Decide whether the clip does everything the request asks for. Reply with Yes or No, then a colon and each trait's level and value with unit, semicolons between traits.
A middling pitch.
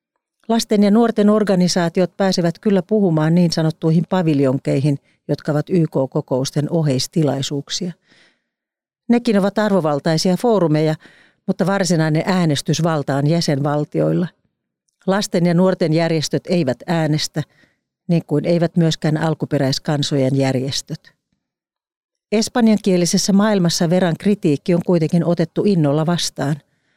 Yes: medium, 170 Hz